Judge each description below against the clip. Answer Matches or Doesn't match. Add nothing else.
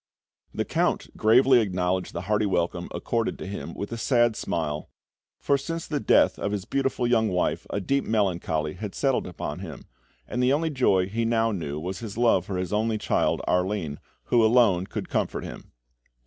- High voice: Doesn't match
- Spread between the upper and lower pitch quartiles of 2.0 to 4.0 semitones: Doesn't match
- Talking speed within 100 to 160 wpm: Doesn't match